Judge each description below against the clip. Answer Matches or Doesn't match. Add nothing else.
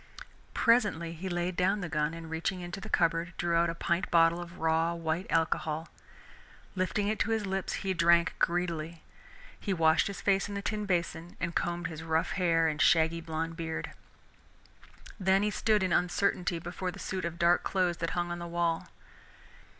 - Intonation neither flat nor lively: Doesn't match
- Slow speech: Doesn't match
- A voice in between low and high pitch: Matches